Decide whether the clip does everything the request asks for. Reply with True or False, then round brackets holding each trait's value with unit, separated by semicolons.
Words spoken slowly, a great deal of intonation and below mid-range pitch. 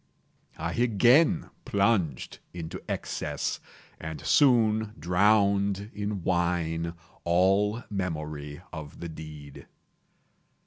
False (85 wpm; 4.5 semitones; 90 Hz)